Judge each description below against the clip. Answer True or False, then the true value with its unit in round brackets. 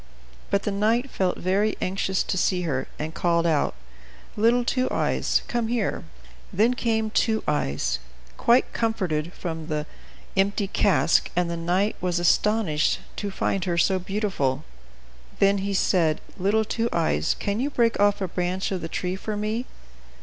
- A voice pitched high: True (195 Hz)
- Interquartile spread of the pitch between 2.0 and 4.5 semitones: True (4.1 semitones)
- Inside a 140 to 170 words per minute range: True (160 wpm)